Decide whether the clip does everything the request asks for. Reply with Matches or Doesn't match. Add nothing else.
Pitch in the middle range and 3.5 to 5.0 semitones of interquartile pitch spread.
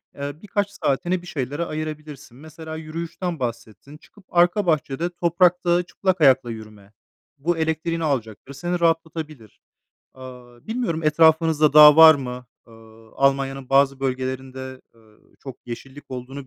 Matches